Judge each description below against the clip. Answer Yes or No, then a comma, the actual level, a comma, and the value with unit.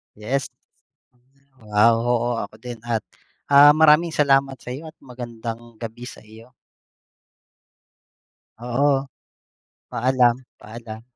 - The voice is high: No, low, 120 Hz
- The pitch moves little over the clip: No, average, 3.0 semitones